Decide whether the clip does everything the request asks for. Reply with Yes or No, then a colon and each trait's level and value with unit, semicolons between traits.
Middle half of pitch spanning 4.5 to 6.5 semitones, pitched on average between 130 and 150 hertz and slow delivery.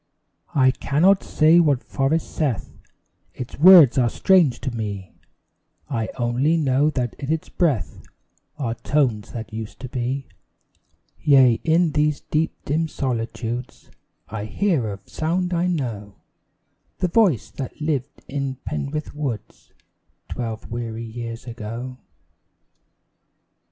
Yes: average, 4.8 semitones; low, 135 Hz; slow, 120 wpm